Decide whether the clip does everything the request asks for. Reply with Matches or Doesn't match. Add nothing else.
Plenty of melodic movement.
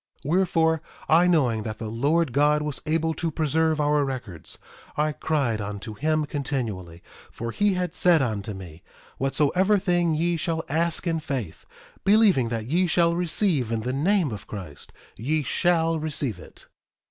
Matches